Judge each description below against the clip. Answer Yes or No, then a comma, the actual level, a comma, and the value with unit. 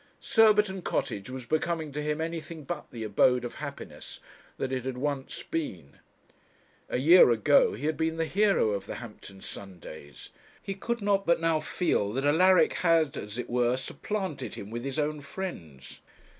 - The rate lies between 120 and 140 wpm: No, average, 170 wpm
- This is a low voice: No, medium, 145 Hz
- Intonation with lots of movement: Yes, wide, 6.0 semitones